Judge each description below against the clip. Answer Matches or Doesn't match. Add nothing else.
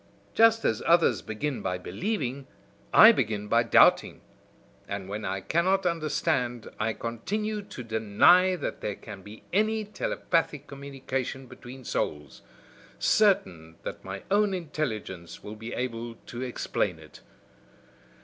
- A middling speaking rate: Doesn't match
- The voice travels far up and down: Matches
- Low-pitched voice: Matches